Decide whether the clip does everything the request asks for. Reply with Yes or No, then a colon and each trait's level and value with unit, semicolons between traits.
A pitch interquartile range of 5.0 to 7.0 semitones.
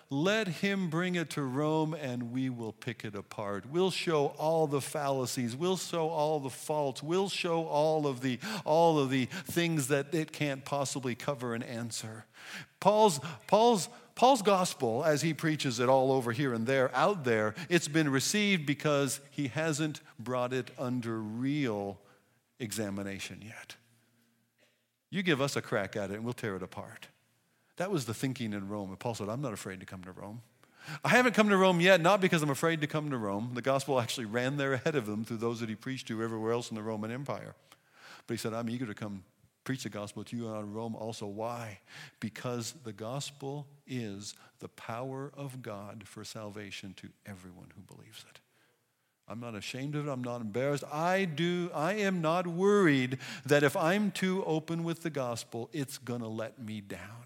Yes: wide, 5.5 semitones